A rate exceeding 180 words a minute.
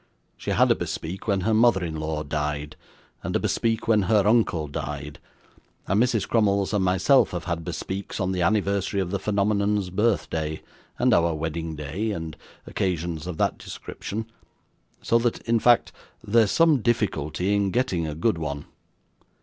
No: average, 165 wpm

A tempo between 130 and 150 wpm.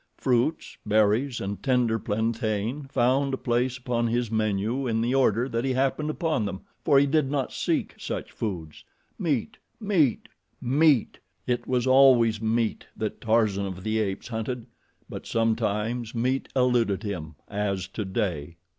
Yes: average, 145 wpm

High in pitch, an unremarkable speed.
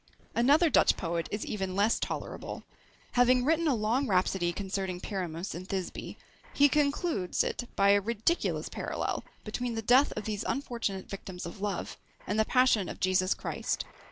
Yes: high, 210 Hz; average, 160 wpm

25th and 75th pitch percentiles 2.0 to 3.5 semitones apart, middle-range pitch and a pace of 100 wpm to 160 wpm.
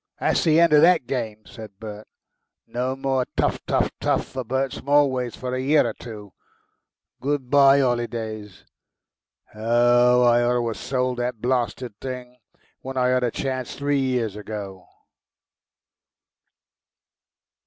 No: narrow, 2.5 semitones; low, 125 Hz; average, 140 wpm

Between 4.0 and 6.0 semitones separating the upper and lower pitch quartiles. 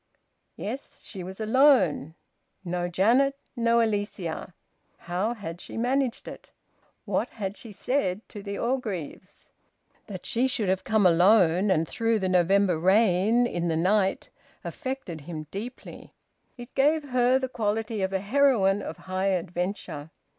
Yes: average, 4.6 semitones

